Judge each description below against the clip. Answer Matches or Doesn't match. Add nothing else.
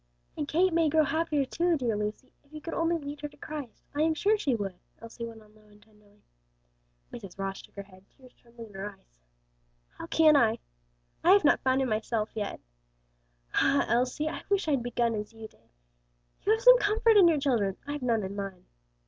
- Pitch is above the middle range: Matches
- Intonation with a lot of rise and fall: Matches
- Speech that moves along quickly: Matches